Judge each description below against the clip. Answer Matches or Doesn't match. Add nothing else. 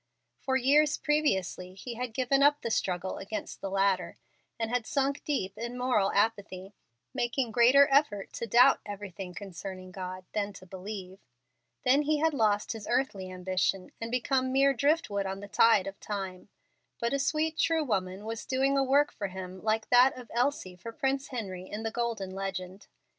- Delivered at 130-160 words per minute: Doesn't match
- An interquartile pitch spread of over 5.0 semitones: Matches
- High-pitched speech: Matches